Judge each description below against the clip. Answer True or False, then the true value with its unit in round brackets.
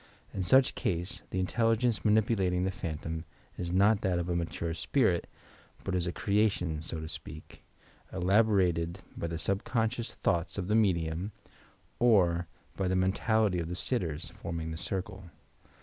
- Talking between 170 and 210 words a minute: False (155 wpm)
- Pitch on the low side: True (90 Hz)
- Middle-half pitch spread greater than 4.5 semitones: False (3.9 semitones)